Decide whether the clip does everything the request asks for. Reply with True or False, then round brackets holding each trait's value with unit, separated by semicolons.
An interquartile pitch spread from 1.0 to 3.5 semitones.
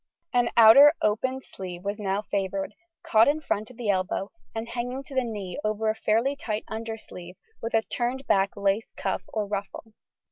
True (3.0 semitones)